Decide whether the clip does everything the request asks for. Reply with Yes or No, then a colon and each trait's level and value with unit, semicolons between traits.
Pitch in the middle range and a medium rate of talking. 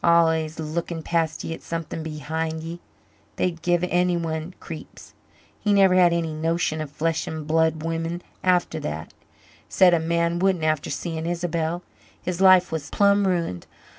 Yes: medium, 165 Hz; average, 155 wpm